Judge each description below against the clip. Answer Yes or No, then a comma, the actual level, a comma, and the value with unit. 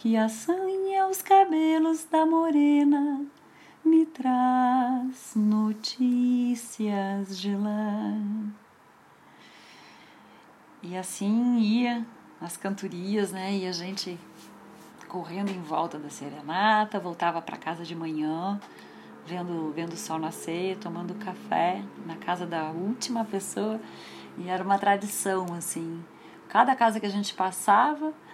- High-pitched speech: Yes, high, 205 Hz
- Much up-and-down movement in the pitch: Yes, wide, 5.8 semitones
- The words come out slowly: Yes, slow, 110 wpm